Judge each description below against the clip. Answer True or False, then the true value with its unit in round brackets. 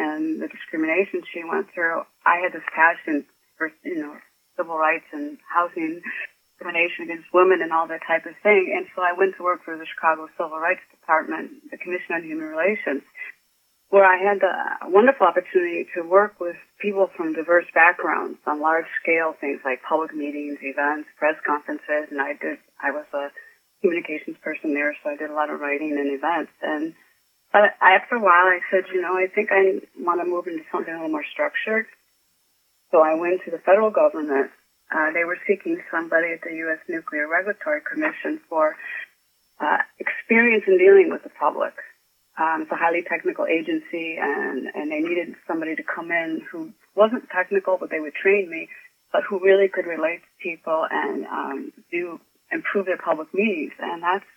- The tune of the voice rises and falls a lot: True (6.9 semitones)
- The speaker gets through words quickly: False (185 wpm)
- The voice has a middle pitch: True (175 Hz)